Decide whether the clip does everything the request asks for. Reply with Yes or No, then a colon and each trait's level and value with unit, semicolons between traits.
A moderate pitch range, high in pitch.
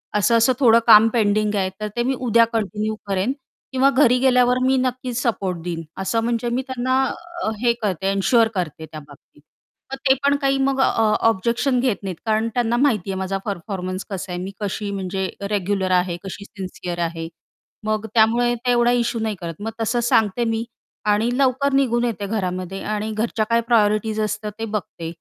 Yes: average, 3.8 semitones; high, 220 Hz